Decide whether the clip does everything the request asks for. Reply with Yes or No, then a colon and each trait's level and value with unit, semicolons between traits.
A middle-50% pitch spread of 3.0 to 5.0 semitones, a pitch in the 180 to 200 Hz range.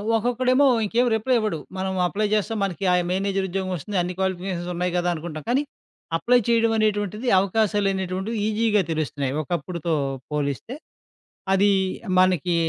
Yes: average, 3.5 semitones; high, 195 Hz